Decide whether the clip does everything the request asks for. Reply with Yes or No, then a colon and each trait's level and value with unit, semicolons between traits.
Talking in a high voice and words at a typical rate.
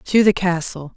No: medium, 180 Hz; average, 190 wpm